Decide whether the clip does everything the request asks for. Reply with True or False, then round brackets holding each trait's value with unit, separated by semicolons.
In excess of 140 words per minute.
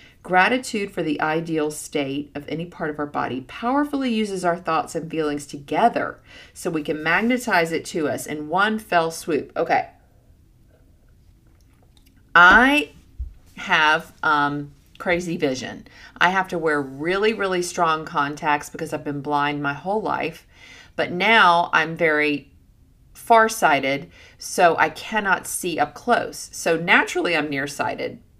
False (135 wpm)